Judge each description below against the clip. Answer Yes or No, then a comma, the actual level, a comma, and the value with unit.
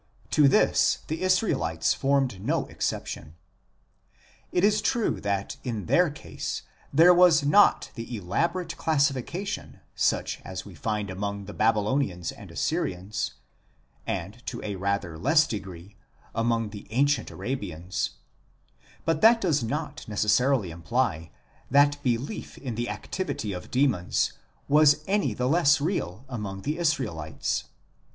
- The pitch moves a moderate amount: No, wide, 7.2 semitones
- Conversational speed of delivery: No, slow, 130 wpm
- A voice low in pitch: Yes, low, 125 Hz